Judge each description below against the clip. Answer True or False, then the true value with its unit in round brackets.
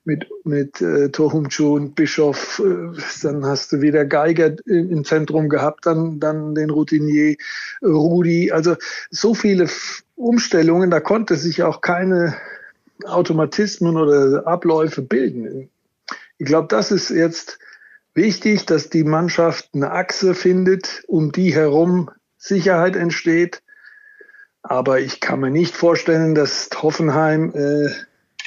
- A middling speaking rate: False (120 wpm)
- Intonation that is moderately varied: True (3.1 semitones)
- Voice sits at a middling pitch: True (165 Hz)